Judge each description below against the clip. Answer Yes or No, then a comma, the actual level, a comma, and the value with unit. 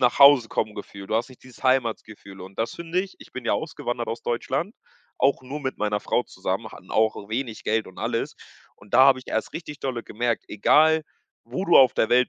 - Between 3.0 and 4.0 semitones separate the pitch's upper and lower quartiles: Yes, average, 3.7 semitones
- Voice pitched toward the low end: Yes, low, 120 Hz